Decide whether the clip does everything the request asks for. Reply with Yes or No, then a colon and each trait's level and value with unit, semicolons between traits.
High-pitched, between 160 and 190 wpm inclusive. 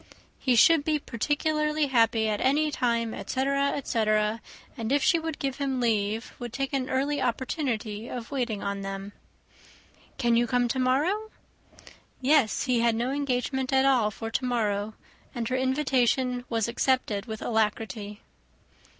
No: very high, 250 Hz; average, 150 wpm